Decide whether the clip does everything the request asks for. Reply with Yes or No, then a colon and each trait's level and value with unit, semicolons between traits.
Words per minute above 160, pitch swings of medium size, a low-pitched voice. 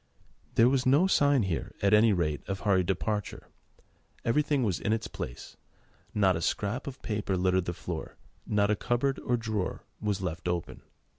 Yes: average, 170 wpm; average, 4.7 semitones; low, 105 Hz